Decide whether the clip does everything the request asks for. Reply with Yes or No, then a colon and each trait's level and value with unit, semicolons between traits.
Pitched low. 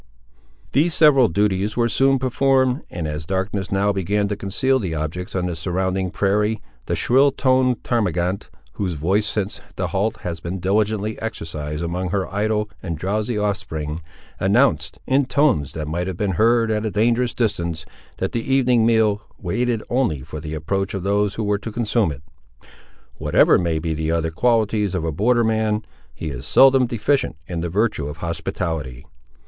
Yes: low, 100 Hz